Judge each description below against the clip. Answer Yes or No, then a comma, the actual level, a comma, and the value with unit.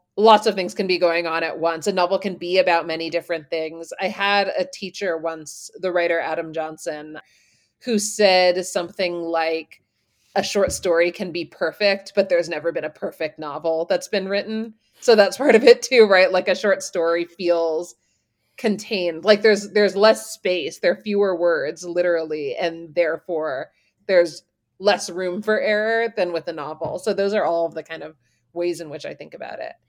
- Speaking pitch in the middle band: Yes, medium, 175 Hz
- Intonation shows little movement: No, average, 3.5 semitones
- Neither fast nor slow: Yes, average, 190 wpm